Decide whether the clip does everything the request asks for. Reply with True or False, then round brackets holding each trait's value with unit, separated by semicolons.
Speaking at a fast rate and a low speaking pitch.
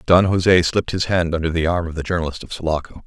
True (255 wpm; 85 Hz)